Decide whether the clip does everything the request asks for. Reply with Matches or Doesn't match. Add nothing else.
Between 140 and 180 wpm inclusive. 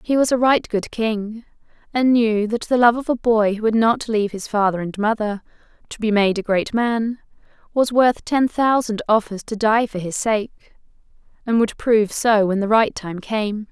Doesn't match